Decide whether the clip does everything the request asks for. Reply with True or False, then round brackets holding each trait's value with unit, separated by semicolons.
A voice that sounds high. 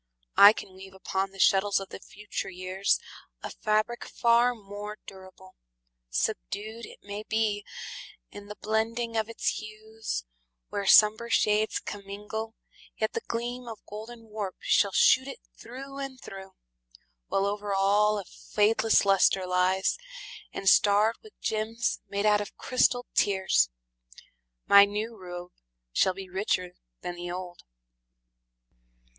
True (205 Hz)